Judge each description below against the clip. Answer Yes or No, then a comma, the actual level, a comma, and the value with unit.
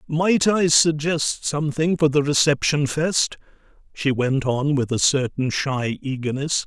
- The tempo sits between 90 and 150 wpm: Yes, average, 145 wpm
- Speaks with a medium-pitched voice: Yes, medium, 145 Hz